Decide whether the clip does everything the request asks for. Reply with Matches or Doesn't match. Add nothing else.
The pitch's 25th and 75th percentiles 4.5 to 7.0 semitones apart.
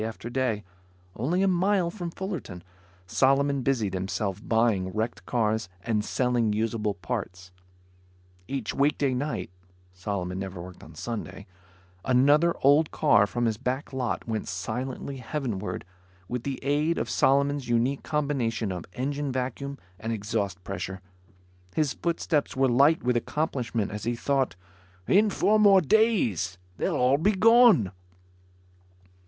Matches